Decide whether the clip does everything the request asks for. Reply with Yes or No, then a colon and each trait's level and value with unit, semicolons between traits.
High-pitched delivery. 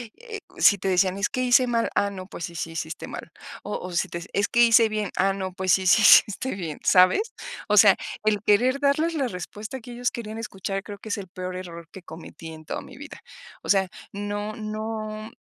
Yes: high, 205 Hz